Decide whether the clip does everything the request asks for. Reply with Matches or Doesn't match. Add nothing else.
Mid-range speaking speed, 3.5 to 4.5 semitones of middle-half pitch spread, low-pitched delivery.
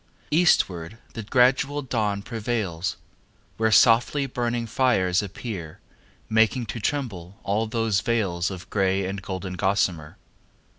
Doesn't match